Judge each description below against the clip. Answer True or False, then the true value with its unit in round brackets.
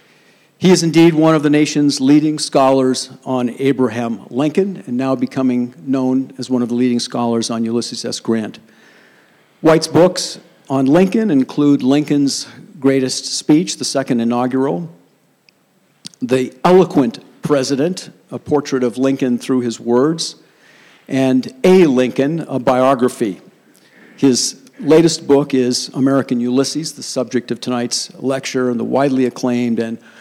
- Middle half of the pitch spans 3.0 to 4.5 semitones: True (3.4 semitones)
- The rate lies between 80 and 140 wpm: True (135 wpm)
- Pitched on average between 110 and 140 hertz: True (135 Hz)